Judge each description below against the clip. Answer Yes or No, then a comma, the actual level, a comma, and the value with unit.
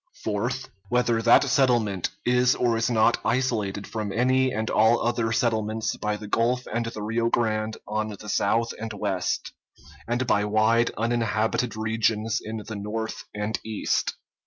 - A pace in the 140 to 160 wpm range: Yes, average, 155 wpm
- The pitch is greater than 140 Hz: No, low, 110 Hz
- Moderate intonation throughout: No, narrow, 1.7 semitones